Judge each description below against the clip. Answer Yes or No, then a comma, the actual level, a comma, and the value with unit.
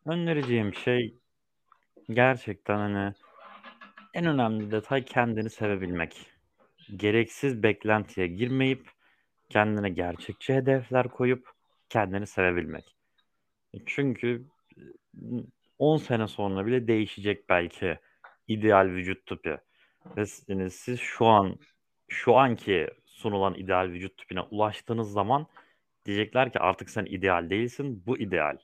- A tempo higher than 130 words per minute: No, average, 105 wpm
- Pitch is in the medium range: No, low, 110 Hz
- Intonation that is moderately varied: Yes, average, 4.2 semitones